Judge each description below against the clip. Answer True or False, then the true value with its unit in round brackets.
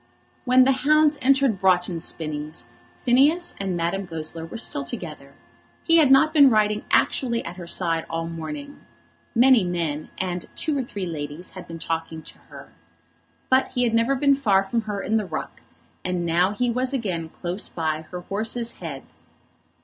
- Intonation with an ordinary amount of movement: False (7.4 semitones)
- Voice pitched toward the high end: True (195 Hz)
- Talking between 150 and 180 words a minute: True (175 wpm)